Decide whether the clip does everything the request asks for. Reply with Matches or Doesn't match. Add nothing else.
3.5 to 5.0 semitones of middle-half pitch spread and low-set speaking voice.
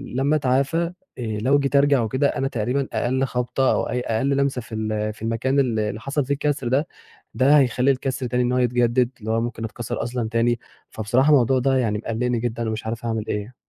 Doesn't match